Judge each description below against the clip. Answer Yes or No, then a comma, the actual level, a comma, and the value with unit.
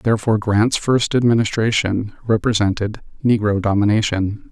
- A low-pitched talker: Yes, low, 110 Hz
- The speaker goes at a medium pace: No, slow, 95 wpm